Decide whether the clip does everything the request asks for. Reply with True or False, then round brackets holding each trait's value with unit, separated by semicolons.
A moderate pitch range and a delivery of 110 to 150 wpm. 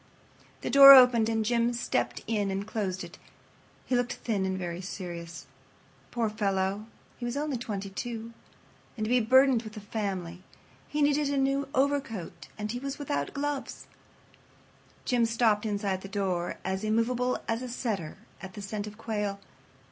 False (4.1 semitones; 165 wpm)